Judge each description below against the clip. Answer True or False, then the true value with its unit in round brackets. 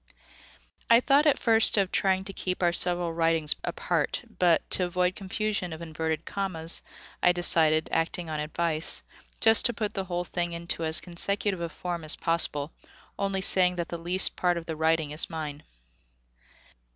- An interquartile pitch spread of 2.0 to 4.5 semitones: True (2.6 semitones)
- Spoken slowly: False (170 wpm)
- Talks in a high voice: False (175 Hz)